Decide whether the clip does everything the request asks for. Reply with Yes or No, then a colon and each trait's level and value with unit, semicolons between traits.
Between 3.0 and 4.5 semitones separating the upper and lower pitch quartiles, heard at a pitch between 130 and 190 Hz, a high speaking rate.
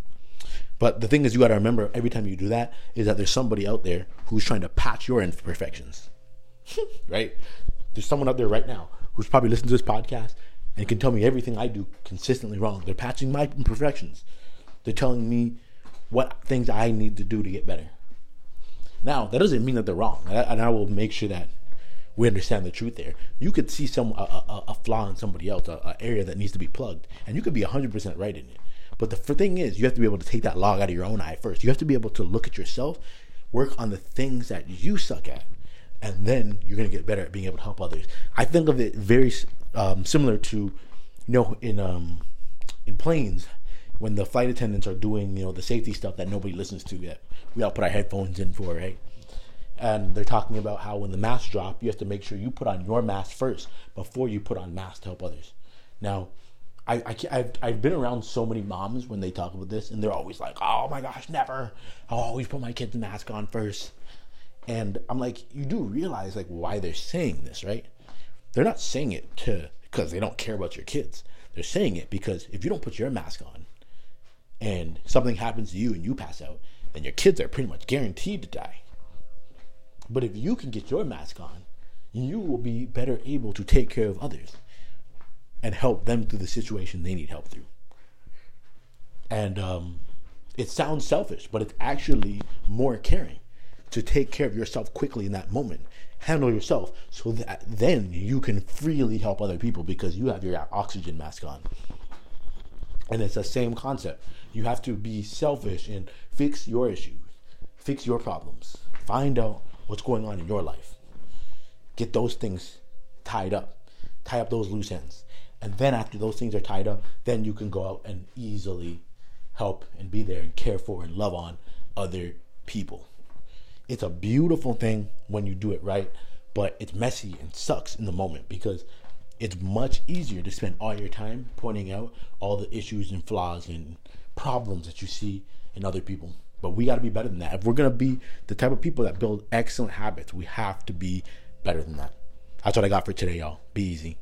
No: average, 4.1 semitones; low, 105 Hz; fast, 215 wpm